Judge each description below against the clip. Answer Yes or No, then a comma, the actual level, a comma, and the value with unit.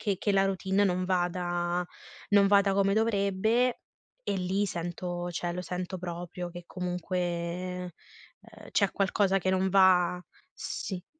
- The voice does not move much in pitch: Yes, narrow, 1.8 semitones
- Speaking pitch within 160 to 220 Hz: Yes, medium, 185 Hz